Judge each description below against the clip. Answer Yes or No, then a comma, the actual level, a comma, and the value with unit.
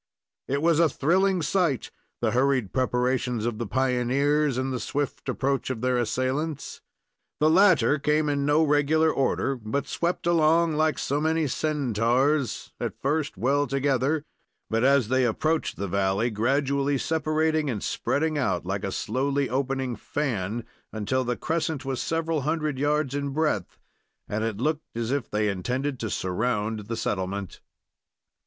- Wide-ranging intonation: No, average, 3.9 semitones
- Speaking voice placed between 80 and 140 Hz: Yes, low, 135 Hz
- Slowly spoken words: No, average, 150 wpm